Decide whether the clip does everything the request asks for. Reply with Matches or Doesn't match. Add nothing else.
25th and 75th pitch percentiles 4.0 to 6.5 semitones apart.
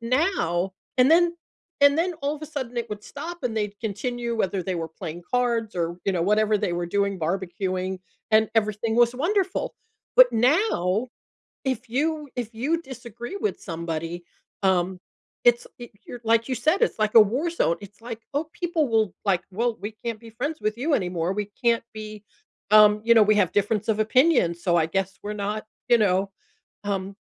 Matches